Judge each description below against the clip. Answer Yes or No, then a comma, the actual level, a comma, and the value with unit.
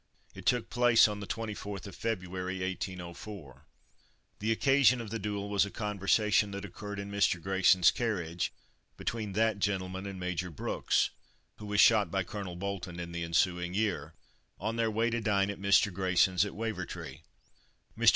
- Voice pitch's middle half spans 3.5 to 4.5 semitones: No, average, 2.7 semitones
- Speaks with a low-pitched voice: Yes, low, 100 Hz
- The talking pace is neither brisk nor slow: Yes, average, 165 wpm